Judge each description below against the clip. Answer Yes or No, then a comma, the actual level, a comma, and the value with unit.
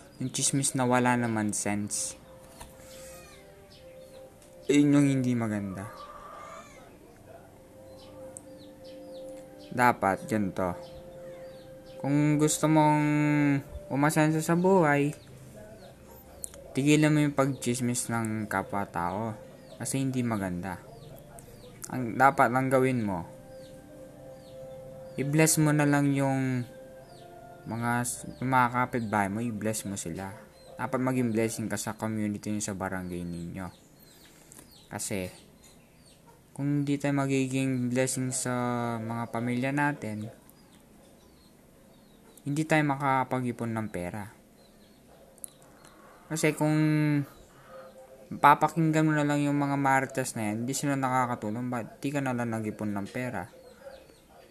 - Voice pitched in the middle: No, low, 130 Hz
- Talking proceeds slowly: Yes, slow, 100 wpm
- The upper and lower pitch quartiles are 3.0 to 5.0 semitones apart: Yes, average, 4.7 semitones